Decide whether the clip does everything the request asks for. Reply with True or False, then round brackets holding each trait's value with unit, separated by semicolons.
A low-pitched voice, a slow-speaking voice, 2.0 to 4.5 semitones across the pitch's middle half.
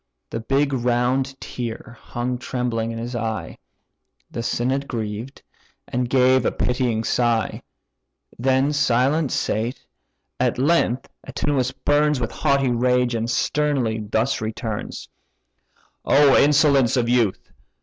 True (125 Hz; 115 wpm; 2.6 semitones)